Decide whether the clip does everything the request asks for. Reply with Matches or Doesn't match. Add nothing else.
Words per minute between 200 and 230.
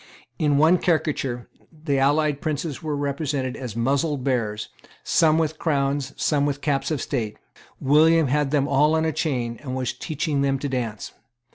Doesn't match